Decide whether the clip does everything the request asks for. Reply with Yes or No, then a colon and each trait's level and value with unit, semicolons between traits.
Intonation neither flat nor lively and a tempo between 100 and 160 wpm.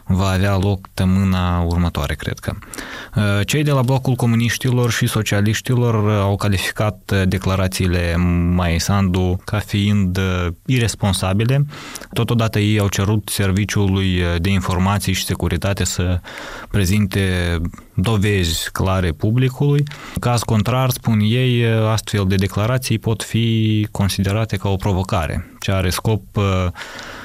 Yes: average, 3.1 semitones; slow, 115 wpm